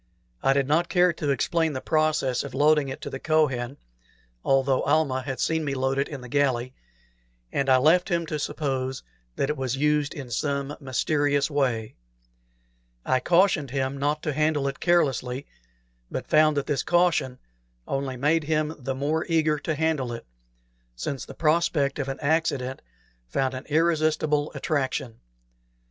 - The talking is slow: No, average, 160 wpm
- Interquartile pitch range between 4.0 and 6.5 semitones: No, average, 2.7 semitones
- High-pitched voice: No, medium, 145 Hz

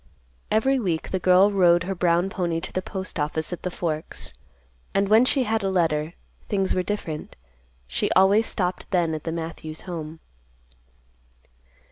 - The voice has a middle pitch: Yes, medium, 180 Hz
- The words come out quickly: No, average, 155 wpm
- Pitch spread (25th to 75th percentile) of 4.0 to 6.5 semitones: No, average, 3.0 semitones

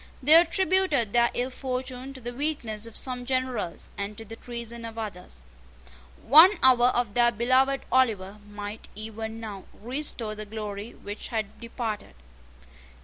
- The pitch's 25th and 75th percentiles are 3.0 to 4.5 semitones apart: Yes, average, 3.3 semitones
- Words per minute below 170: Yes, average, 145 wpm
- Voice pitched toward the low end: No, high, 235 Hz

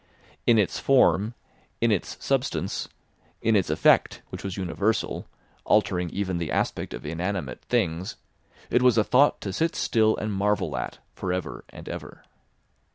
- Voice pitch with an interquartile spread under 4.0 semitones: Yes, average, 3.6 semitones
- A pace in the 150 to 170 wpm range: Yes, average, 155 wpm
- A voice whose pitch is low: Yes, low, 100 Hz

